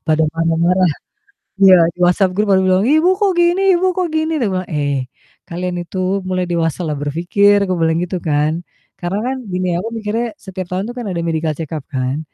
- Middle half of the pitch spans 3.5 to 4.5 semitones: Yes, average, 4.0 semitones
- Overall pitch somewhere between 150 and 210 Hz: Yes, medium, 185 Hz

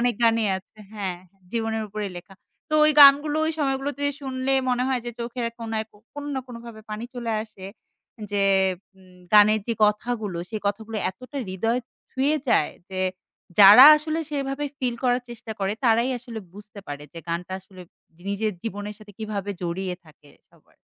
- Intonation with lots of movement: No, average, 3.7 semitones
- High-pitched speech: Yes, high, 225 Hz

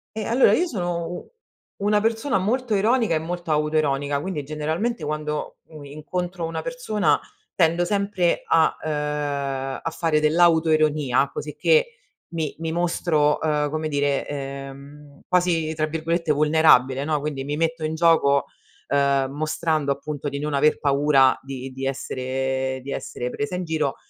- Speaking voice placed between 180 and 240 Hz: No, medium, 155 Hz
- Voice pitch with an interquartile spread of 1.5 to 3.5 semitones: Yes, average, 3.2 semitones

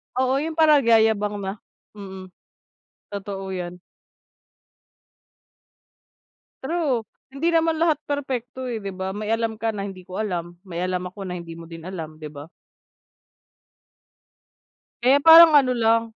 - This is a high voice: Yes, high, 215 Hz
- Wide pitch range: Yes, wide, 6.2 semitones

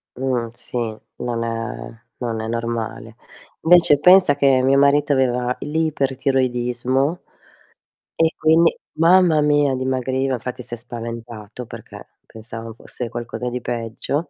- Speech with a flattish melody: No, average, 3.4 semitones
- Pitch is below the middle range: Yes, low, 125 Hz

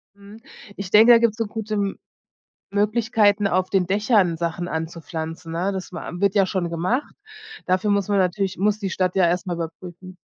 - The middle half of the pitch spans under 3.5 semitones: Yes, average, 2.7 semitones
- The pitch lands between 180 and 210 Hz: Yes, high, 190 Hz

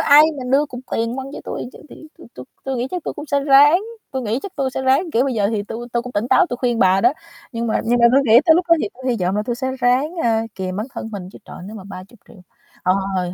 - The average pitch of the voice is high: Yes, high, 245 Hz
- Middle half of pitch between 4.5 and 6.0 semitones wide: No, average, 3.8 semitones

